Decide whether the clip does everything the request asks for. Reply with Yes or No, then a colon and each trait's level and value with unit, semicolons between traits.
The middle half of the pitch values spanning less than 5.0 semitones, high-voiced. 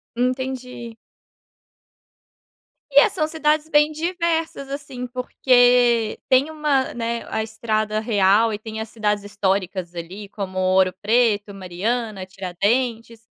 Yes: average, 4.3 semitones; high, 230 Hz